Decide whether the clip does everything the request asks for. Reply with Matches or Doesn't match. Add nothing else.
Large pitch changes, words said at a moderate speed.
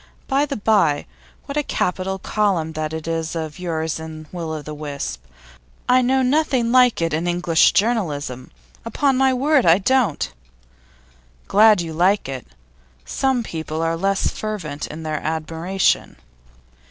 Matches